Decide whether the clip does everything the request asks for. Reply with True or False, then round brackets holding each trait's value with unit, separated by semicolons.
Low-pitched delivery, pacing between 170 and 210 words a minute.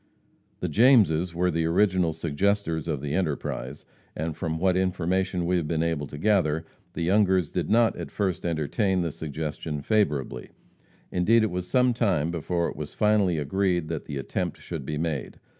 True (85 Hz; 175 wpm)